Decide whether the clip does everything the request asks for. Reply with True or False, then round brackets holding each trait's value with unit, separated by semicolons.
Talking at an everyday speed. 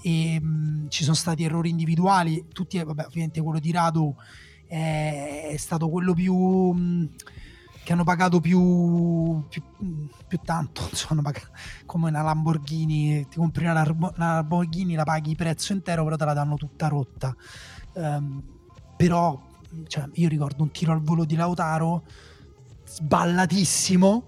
True (145 wpm)